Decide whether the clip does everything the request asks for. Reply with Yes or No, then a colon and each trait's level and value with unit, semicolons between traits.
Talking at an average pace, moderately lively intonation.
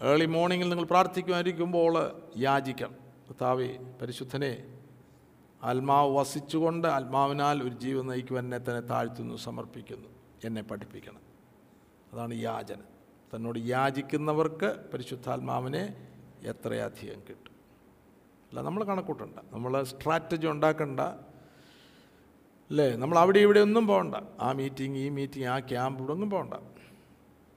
Yes: average, 100 wpm; average, 4.4 semitones